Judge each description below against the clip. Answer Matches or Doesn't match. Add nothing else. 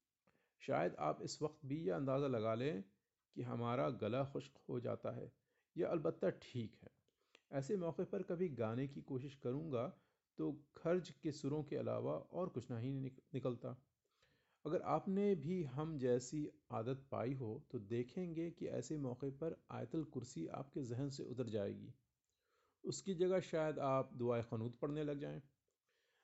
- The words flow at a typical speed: Matches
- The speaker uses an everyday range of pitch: Matches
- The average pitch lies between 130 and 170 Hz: Matches